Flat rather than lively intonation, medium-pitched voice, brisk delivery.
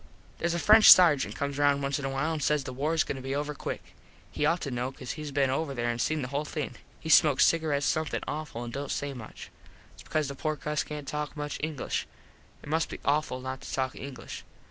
Yes: narrow, 2.3 semitones; medium, 145 Hz; fast, 245 wpm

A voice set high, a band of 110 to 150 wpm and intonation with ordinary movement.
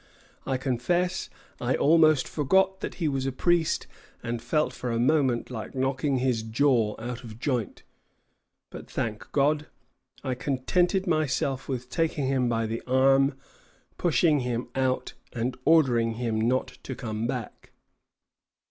No: low, 130 Hz; average, 140 wpm; average, 3.8 semitones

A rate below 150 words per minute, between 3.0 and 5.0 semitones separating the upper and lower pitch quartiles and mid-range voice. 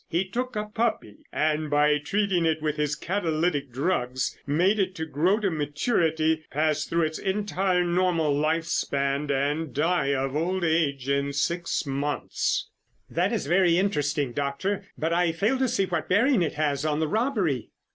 No: average, 165 wpm; average, 4.2 semitones; medium, 160 Hz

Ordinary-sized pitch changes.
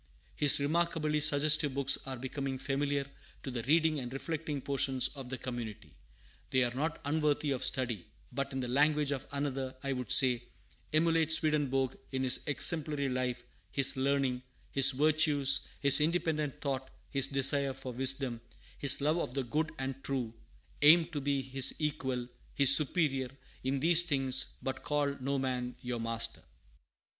No: narrow, 2.2 semitones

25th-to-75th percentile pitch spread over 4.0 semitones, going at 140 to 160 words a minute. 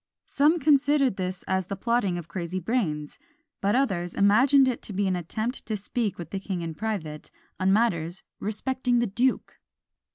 No: wide, 5.4 semitones; average, 170 wpm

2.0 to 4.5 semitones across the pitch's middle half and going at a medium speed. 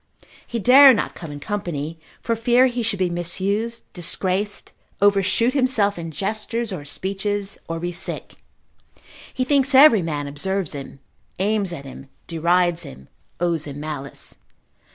No: average, 5.2 semitones; average, 145 wpm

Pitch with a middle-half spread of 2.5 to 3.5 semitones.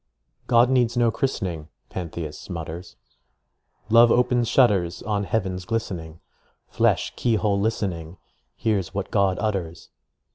No: average, 4.9 semitones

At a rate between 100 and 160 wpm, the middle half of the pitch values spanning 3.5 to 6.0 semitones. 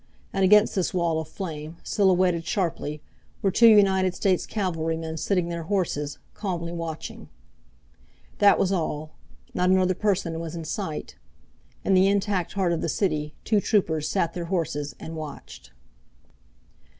No: average, 145 wpm; average, 3.1 semitones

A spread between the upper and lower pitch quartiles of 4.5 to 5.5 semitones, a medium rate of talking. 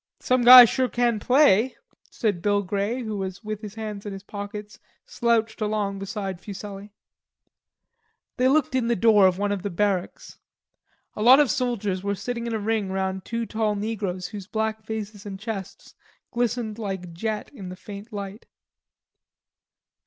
No: narrow, 2.6 semitones; average, 160 wpm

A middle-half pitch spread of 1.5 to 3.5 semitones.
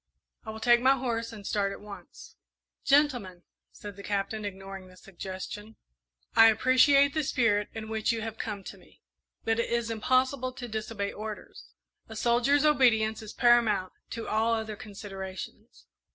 Yes: average, 2.8 semitones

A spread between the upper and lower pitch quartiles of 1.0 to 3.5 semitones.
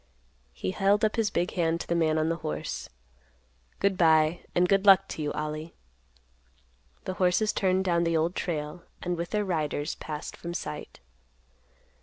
Yes: average, 3.1 semitones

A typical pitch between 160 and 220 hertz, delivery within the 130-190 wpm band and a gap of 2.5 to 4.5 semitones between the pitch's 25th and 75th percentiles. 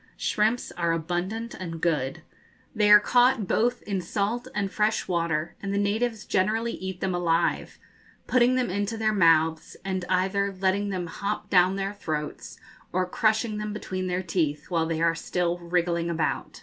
Yes: high, 190 Hz; average, 165 wpm; average, 3.7 semitones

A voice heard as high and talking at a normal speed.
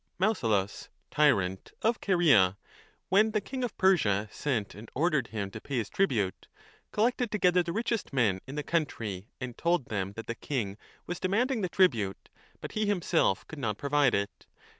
No: medium, 140 Hz; average, 180 wpm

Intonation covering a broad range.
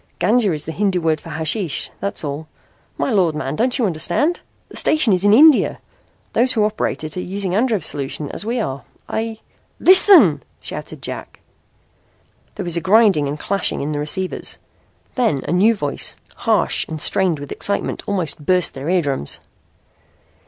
Yes: wide, 6.1 semitones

